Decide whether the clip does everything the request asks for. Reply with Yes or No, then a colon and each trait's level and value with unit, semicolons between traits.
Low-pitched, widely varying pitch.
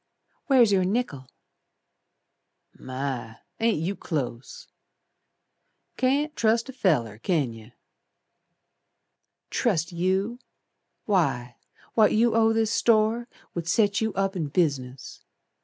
No: high, 190 Hz; wide, 8.4 semitones